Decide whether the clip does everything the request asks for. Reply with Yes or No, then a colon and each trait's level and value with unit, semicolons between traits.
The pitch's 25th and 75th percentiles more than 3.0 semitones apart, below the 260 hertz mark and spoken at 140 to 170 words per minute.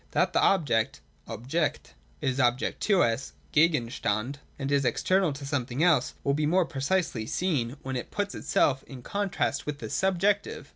No: wide, 5.6 semitones; medium, 140 Hz; average, 180 wpm